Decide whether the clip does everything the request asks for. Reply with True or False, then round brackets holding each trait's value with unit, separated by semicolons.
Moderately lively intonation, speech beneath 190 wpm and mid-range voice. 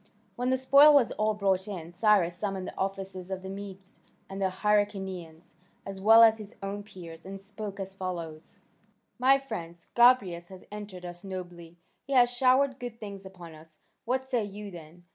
False (3.4 semitones; 180 wpm; 195 Hz)